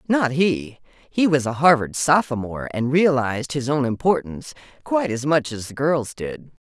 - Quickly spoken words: No, average, 170 wpm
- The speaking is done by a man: No, female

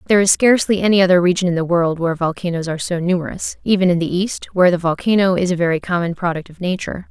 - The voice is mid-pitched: Yes, medium, 180 Hz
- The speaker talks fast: Yes, fast, 235 wpm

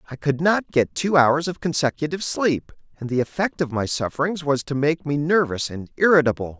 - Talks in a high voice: No, medium, 150 Hz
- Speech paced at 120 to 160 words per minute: No, average, 200 wpm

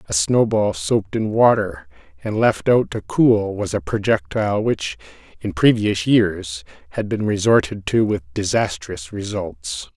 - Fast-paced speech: No, average, 150 wpm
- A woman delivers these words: No, male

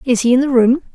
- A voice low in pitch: No, very high, 255 Hz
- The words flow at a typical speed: No, fast, 315 wpm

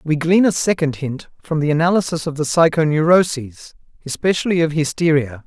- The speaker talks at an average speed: Yes, average, 155 wpm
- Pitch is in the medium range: Yes, medium, 155 Hz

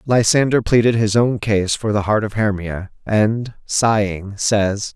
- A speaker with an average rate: Yes, average, 155 wpm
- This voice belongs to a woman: No, male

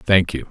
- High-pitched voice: No, very low, 85 Hz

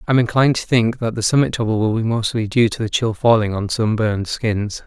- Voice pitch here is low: Yes, low, 115 Hz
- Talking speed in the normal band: No, fast, 235 wpm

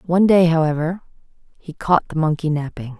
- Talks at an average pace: Yes, average, 160 wpm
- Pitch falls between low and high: Yes, medium, 165 Hz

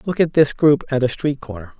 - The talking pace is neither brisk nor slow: No, fast, 270 wpm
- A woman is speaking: No, male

